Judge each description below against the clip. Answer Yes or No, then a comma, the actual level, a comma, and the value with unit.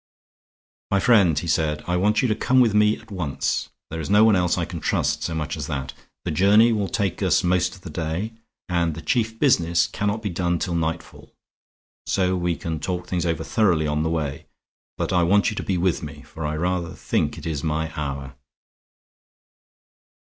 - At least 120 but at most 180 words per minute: No, fast, 205 wpm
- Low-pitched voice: Yes, very low, 85 Hz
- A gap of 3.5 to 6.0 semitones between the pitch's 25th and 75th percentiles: Yes, average, 4.1 semitones